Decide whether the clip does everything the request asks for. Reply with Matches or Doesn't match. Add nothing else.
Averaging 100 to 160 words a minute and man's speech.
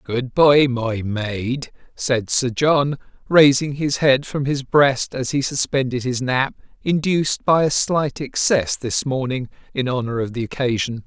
Matches